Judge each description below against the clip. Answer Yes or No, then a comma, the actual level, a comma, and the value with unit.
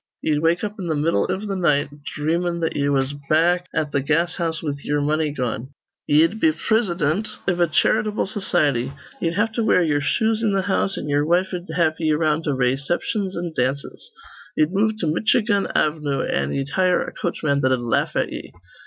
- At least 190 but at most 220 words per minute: Yes, average, 195 wpm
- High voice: No, medium, 165 Hz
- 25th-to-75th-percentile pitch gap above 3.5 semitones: Yes, average, 4.4 semitones